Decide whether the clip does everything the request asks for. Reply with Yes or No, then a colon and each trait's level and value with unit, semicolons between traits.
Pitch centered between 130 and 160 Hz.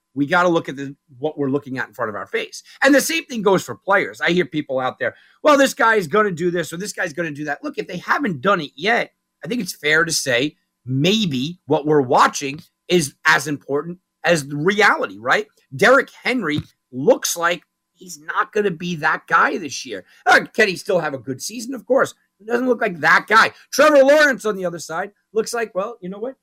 No: medium, 175 Hz